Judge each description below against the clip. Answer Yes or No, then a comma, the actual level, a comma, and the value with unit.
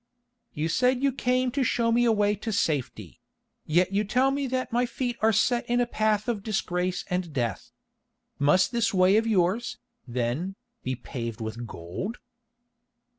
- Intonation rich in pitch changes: Yes, wide, 6.5 semitones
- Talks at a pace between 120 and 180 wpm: Yes, average, 165 wpm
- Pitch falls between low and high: No, high, 210 Hz